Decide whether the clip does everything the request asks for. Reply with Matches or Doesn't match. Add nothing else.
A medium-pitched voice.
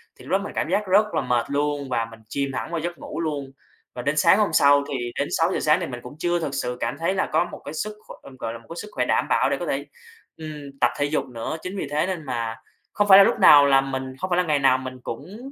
Matches